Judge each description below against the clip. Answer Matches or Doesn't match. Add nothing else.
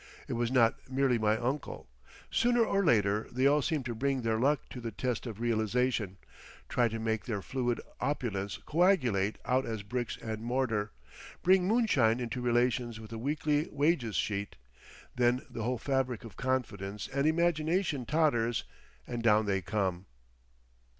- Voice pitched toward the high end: Doesn't match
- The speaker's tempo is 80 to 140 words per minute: Doesn't match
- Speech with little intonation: Doesn't match